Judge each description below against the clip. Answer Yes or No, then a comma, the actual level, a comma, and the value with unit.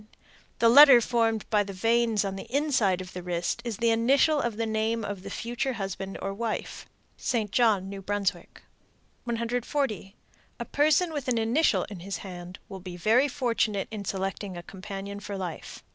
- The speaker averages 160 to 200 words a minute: Yes, average, 175 wpm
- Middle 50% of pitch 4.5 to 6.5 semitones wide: No, average, 3.5 semitones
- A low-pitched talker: No, high, 215 Hz